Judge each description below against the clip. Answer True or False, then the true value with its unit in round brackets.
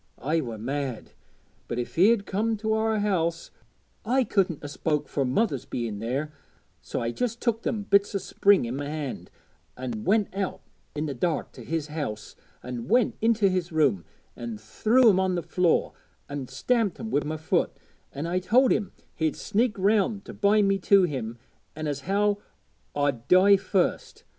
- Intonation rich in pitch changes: True (6.6 semitones)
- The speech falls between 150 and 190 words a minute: True (180 wpm)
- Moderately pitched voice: True (175 Hz)